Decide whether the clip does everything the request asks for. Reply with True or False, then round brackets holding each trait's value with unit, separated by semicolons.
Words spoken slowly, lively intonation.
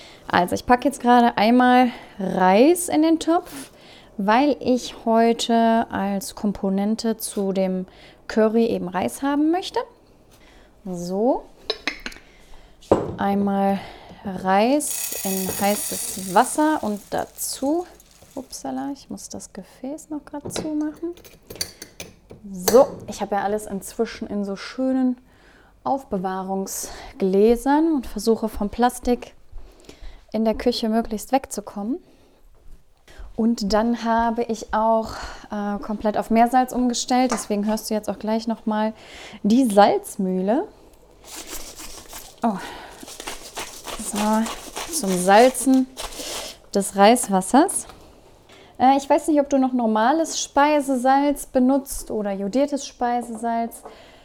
False (105 wpm; 4.5 semitones)